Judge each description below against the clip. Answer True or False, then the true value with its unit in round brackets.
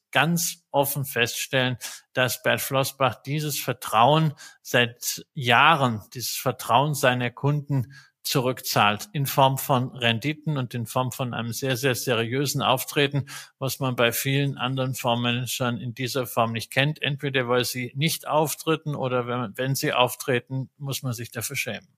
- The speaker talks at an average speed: True (145 wpm)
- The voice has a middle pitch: False (130 Hz)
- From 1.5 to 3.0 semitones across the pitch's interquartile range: True (2.5 semitones)